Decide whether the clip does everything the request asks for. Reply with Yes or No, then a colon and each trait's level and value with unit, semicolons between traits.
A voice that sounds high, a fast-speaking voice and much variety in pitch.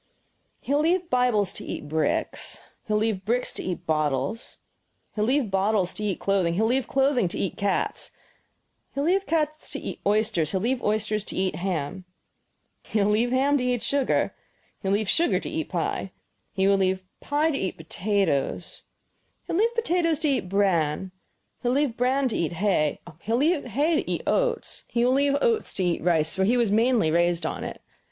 Yes: high, 215 Hz; fast, 210 wpm; wide, 6.5 semitones